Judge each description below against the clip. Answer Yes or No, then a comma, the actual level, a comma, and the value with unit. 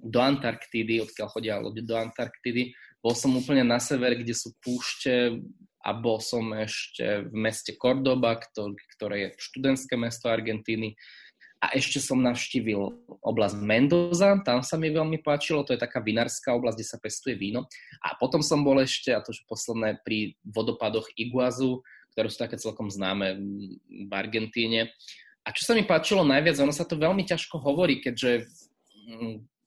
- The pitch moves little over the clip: No, average, 3.3 semitones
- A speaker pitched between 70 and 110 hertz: No, low, 120 Hz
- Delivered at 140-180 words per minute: Yes, average, 160 wpm